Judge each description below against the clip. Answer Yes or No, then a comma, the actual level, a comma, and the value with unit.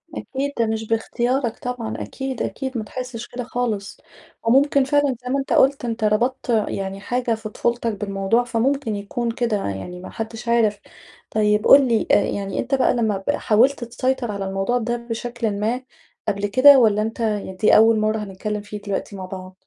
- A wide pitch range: No, average, 3.0 semitones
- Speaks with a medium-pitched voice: No, high, 225 Hz